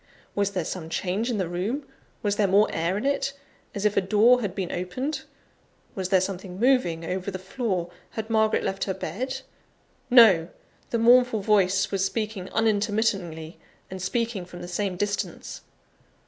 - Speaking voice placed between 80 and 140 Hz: No, high, 200 Hz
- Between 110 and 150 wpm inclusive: No, average, 165 wpm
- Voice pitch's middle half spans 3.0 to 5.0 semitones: Yes, average, 3.5 semitones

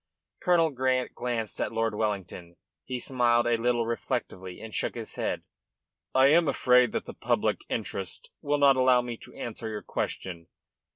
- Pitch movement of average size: Yes, average, 3.0 semitones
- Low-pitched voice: Yes, low, 120 Hz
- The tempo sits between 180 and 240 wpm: No, average, 165 wpm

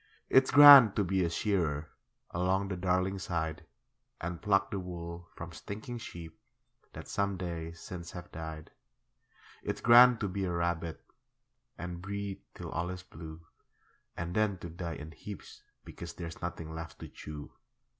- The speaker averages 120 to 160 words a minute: Yes, average, 155 wpm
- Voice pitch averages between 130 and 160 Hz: No, very low, 90 Hz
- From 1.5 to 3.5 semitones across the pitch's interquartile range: Yes, average, 2.9 semitones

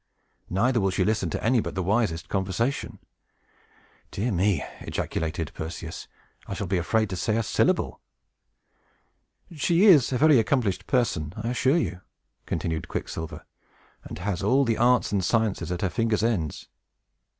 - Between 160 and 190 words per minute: No, average, 150 wpm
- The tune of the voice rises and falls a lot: No, average, 4.9 semitones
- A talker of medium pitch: No, low, 105 Hz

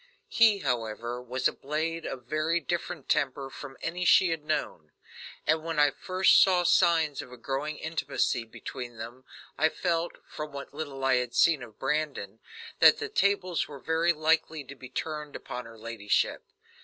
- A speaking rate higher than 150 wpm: Yes, average, 170 wpm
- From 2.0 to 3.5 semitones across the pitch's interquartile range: No, average, 4.7 semitones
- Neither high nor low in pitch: Yes, medium, 150 Hz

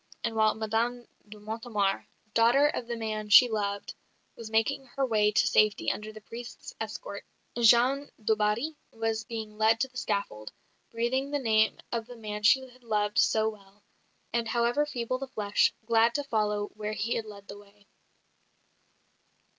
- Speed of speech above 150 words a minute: Yes, average, 170 wpm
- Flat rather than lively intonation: Yes, narrow, 2.2 semitones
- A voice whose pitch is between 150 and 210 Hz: No, high, 225 Hz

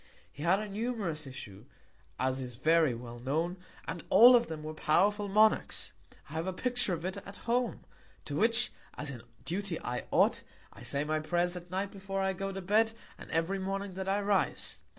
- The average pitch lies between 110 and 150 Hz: No, medium, 185 Hz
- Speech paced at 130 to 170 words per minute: No, average, 195 wpm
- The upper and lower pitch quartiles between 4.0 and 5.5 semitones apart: Yes, average, 4.6 semitones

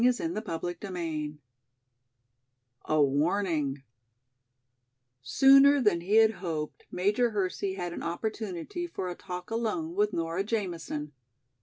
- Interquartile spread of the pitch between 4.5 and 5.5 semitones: Yes, average, 5.2 semitones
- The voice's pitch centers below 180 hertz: No, medium, 185 Hz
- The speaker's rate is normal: No, slow, 110 wpm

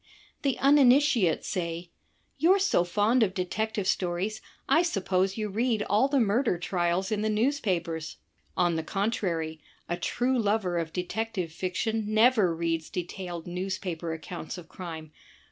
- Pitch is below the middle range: No, high, 190 Hz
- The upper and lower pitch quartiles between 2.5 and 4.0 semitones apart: No, average, 4.5 semitones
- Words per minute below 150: Yes, average, 140 wpm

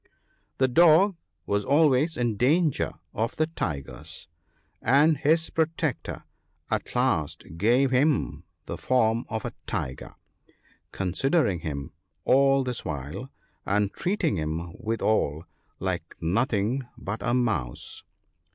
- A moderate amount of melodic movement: No, wide, 7.2 semitones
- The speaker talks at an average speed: No, slow, 115 wpm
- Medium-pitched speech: No, low, 120 Hz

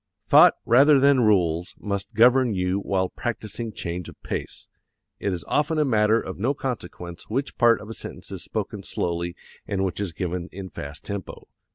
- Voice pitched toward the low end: Yes, low, 100 Hz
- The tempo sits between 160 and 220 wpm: Yes, average, 180 wpm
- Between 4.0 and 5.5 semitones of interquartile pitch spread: Yes, average, 4.7 semitones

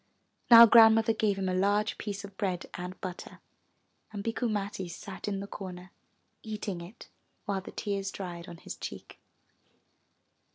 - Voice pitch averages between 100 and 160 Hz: No, high, 200 Hz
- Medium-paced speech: Yes, average, 155 wpm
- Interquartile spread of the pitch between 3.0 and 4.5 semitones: No, narrow, 2.4 semitones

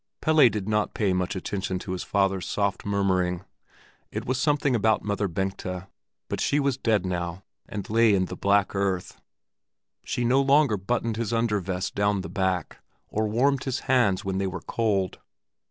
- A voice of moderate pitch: No, low, 100 Hz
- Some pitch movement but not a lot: Yes, average, 3.7 semitones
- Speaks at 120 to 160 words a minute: No, average, 175 wpm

